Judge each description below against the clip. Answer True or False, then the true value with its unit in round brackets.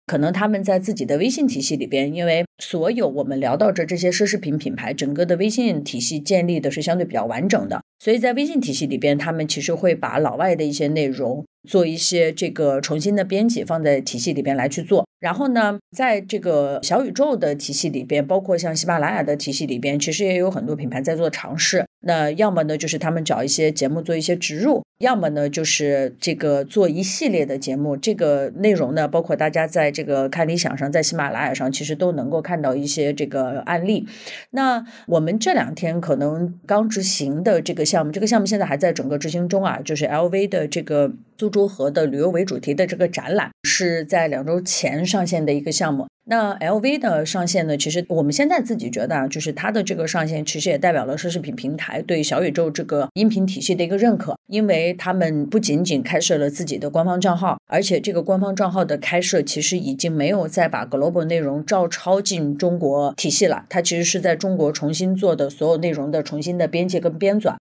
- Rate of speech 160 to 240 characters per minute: False (340 characters per minute)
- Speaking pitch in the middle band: True (170 Hz)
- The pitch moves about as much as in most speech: True (4.4 semitones)